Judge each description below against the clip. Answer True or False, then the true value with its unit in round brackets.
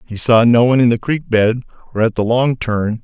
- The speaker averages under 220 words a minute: False (255 wpm)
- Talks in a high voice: False (115 Hz)